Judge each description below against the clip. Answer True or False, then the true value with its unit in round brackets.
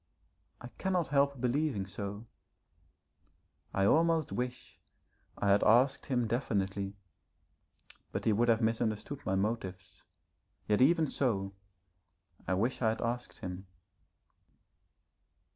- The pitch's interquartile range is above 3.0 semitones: True (5.0 semitones)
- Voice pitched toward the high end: False (115 Hz)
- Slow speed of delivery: True (110 wpm)